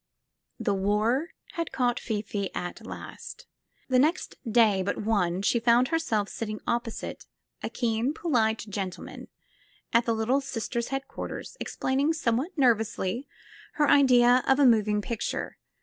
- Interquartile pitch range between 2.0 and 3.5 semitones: No, average, 3.9 semitones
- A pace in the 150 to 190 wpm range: No, average, 140 wpm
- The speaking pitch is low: No, high, 235 Hz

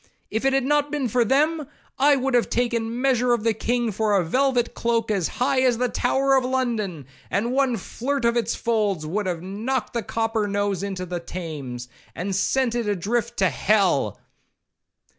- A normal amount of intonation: Yes, average, 4.4 semitones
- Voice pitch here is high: Yes, high, 230 Hz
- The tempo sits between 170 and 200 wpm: Yes, average, 190 wpm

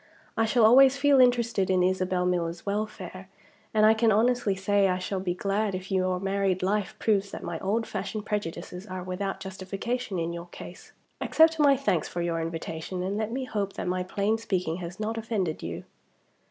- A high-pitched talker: Yes, high, 195 Hz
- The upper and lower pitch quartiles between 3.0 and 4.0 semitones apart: Yes, average, 3.3 semitones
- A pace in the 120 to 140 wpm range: No, average, 190 wpm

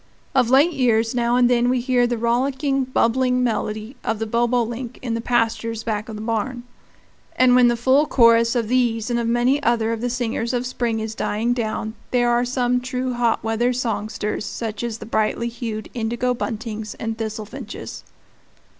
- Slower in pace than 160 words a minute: No, average, 180 wpm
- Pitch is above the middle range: Yes, high, 235 Hz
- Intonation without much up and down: Yes, narrow, 1.8 semitones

